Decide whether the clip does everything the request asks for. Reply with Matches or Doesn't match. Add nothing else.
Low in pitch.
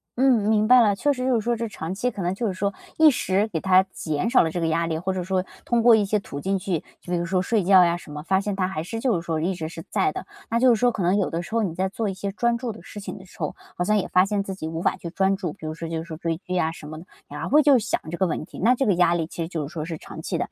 Doesn't match